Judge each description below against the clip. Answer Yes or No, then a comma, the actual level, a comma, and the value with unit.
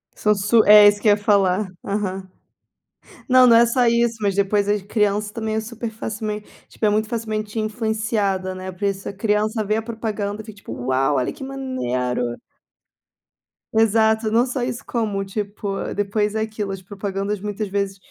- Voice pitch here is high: Yes, high, 210 Hz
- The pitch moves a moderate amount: No, narrow, 1.9 semitones